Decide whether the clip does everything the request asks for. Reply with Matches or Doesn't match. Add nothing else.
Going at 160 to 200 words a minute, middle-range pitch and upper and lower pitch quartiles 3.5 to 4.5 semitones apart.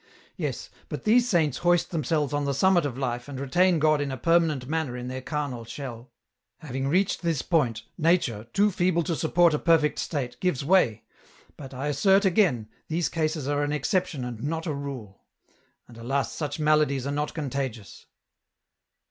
Matches